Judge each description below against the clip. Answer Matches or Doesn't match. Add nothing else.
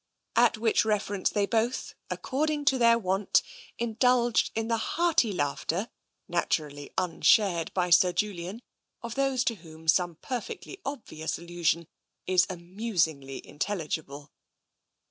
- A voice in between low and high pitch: Doesn't match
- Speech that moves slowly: Matches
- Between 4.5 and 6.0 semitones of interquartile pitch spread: Matches